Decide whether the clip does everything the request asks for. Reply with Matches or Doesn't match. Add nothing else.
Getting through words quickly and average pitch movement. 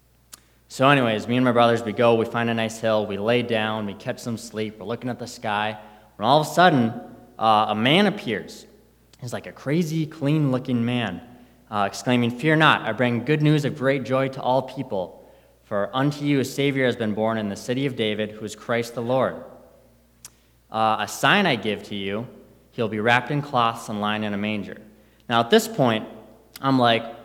Matches